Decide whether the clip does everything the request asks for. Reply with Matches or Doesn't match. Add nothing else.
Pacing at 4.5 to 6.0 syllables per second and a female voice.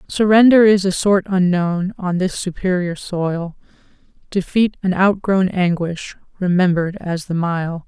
Doesn't match